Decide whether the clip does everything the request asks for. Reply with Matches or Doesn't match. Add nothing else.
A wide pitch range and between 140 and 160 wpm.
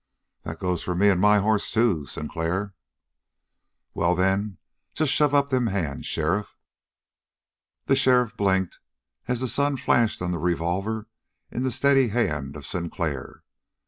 Matches